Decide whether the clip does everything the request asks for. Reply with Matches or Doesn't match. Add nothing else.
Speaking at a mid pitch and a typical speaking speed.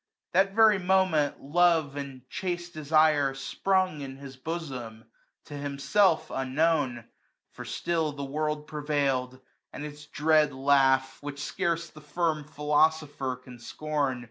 Doesn't match